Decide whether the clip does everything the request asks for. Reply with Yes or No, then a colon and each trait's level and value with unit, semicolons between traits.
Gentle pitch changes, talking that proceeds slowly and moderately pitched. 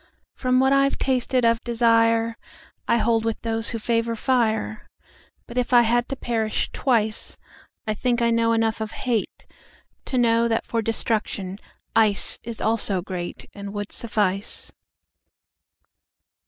No: narrow, 1.6 semitones; slow, 120 wpm; high, 230 Hz